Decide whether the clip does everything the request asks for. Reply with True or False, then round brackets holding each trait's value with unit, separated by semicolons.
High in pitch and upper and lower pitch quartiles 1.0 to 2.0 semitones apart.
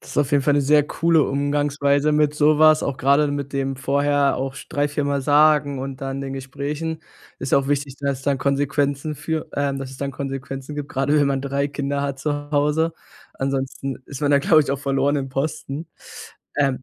False (140 Hz; 1.3 semitones)